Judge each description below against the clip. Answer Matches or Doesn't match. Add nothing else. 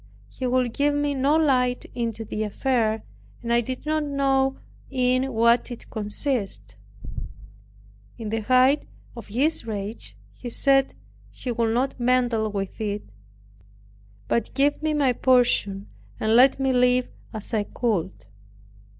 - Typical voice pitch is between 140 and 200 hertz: Doesn't match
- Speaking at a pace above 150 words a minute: Doesn't match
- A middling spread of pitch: Matches